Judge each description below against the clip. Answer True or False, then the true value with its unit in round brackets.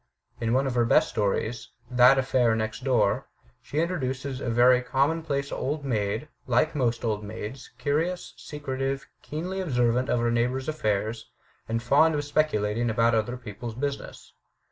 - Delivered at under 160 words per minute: False (165 wpm)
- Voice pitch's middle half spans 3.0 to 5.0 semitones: True (3.6 semitones)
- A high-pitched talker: False (125 Hz)